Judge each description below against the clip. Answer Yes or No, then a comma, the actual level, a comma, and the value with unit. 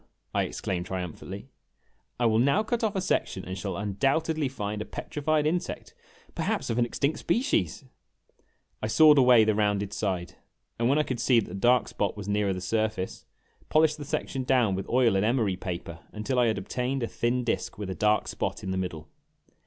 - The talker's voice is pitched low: Yes, low, 110 Hz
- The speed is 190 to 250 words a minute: Yes, average, 195 wpm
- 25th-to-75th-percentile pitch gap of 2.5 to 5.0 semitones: No, wide, 5.5 semitones